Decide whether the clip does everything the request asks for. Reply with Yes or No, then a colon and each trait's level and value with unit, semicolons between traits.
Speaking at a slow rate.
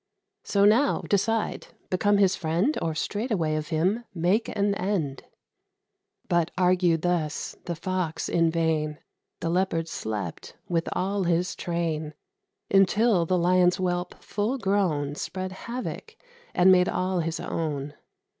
Yes: slow, 130 wpm